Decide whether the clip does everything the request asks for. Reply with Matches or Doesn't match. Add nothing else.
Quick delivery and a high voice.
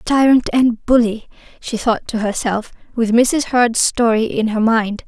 Doesn't match